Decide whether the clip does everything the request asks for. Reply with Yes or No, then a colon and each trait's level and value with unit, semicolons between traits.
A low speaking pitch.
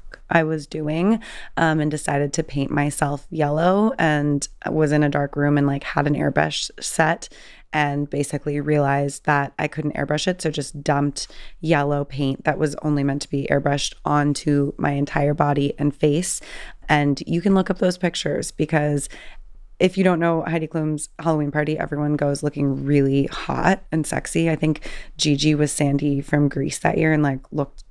No: medium, 150 Hz